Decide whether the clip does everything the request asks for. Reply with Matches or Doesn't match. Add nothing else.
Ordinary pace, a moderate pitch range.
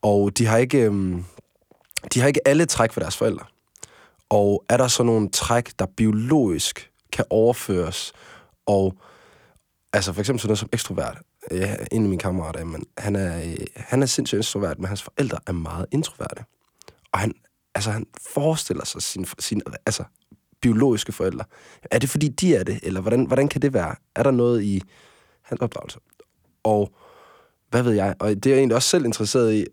Matches